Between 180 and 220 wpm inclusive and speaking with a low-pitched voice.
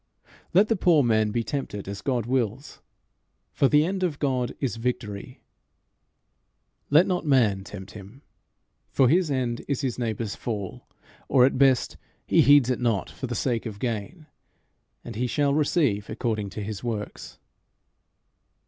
No: average, 155 wpm; low, 125 Hz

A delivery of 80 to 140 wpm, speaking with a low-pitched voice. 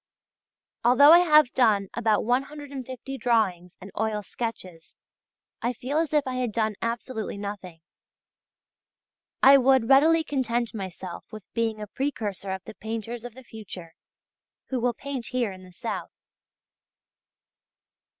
No: slow, 135 wpm; high, 230 Hz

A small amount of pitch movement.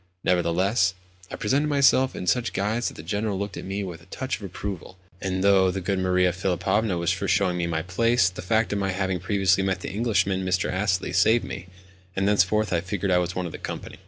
Yes: narrow, 2.2 semitones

